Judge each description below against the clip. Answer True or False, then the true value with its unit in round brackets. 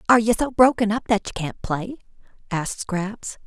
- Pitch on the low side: False (210 Hz)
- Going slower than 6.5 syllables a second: True (5.5 syllables/s)